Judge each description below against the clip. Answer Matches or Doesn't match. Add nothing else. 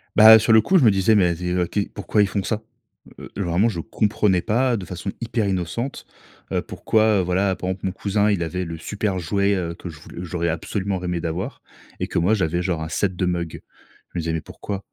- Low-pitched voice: Matches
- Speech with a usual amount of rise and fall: Matches